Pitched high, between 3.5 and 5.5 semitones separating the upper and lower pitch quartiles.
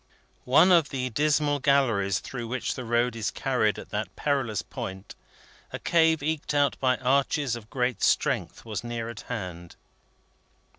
No: low, 125 Hz; average, 3.9 semitones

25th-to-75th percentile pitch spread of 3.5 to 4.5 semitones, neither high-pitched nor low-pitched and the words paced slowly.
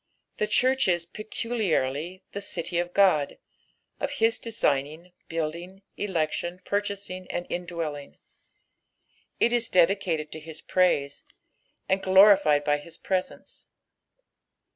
Yes: average, 4.2 semitones; medium, 180 Hz; slow, 120 wpm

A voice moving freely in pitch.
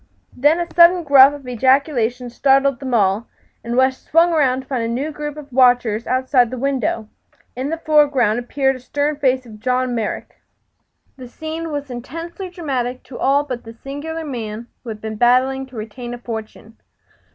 No: average, 3.2 semitones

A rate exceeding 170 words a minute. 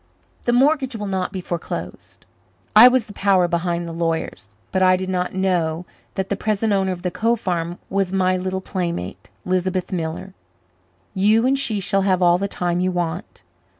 Yes: average, 185 wpm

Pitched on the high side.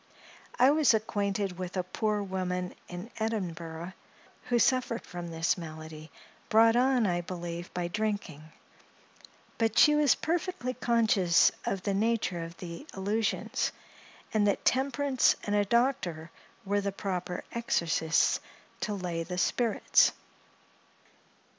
Yes: high, 200 Hz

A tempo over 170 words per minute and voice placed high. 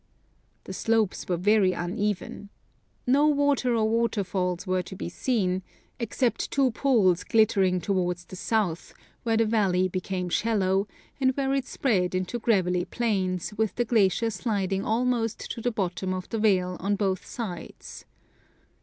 No: average, 150 wpm; high, 205 Hz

